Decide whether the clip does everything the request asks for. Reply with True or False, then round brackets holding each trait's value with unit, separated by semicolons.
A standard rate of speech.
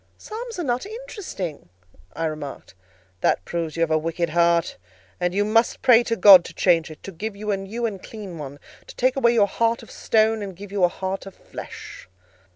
False (210 wpm)